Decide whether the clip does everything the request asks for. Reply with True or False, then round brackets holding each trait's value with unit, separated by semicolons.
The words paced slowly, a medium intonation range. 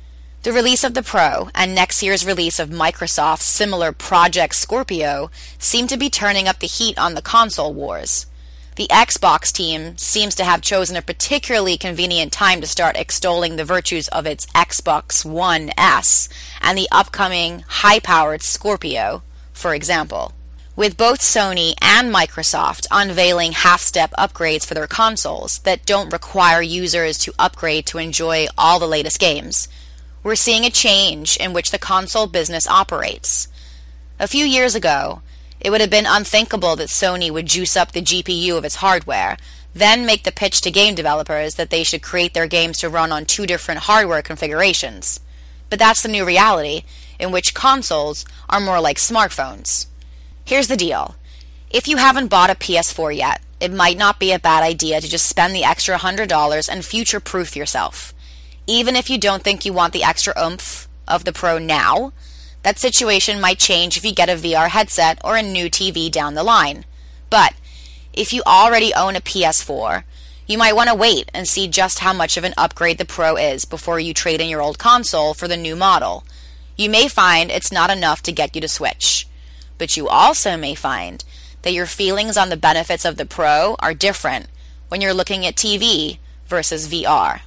False (180 wpm; 4.7 semitones)